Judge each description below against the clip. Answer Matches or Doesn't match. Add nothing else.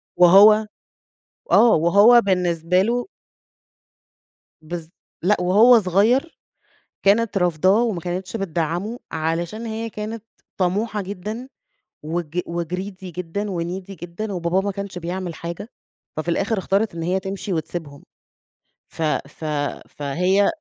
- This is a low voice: Doesn't match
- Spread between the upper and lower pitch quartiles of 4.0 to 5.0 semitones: Doesn't match